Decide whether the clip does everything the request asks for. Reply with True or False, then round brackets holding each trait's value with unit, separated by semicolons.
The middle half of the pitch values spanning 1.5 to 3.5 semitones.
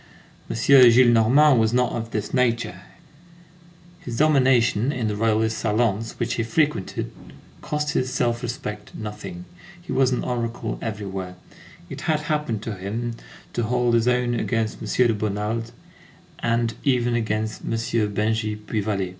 True (2.5 semitones)